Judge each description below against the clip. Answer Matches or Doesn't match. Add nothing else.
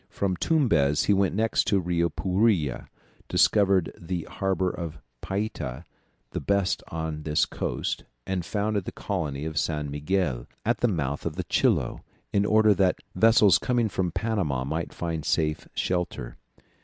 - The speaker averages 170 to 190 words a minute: Doesn't match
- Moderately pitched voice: Doesn't match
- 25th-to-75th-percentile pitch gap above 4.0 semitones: Matches